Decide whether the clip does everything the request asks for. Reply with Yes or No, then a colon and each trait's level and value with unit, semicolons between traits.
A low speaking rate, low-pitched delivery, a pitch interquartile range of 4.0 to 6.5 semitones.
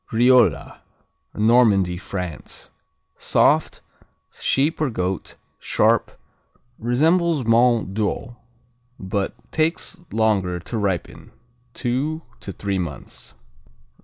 Yes: slow, 85 wpm; low, 110 Hz; average, 5.1 semitones